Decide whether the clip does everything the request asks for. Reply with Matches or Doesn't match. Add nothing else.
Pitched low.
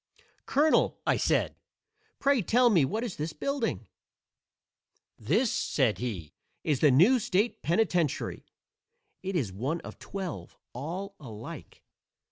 Doesn't match